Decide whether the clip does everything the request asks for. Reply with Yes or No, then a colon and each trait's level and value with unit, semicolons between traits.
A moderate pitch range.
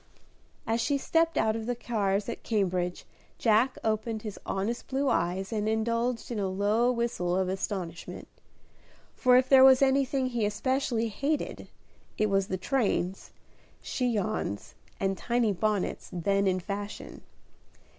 Yes: average, 4.0 semitones